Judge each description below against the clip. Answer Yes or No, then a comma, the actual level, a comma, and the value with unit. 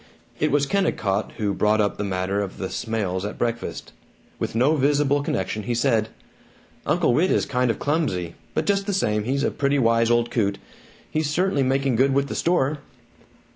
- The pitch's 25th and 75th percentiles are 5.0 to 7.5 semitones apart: Yes, wide, 5.4 semitones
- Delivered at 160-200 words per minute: Yes, average, 185 wpm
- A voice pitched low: Yes, low, 125 Hz